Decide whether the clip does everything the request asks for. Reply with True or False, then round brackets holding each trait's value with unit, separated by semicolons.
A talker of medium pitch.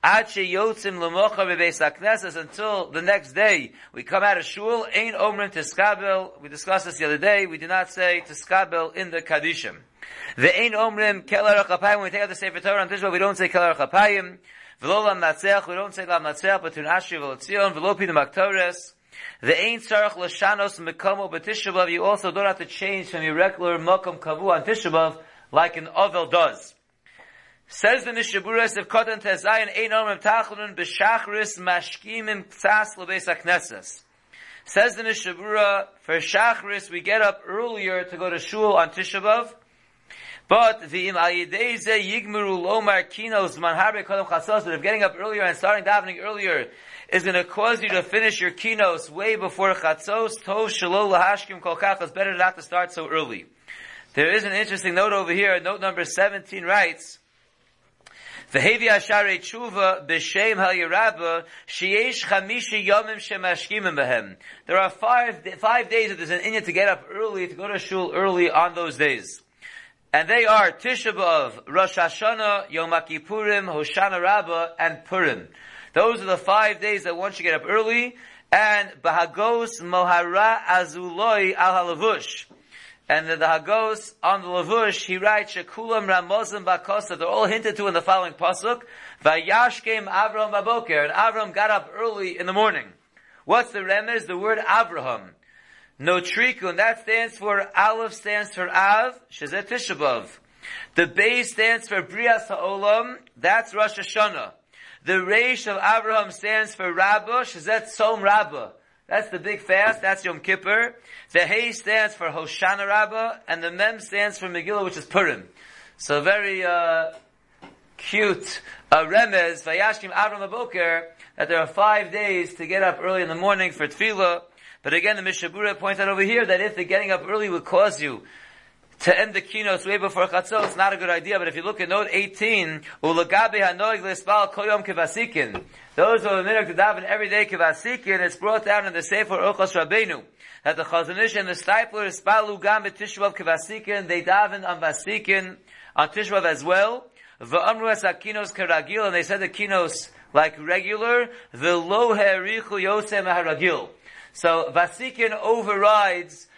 False (195 Hz)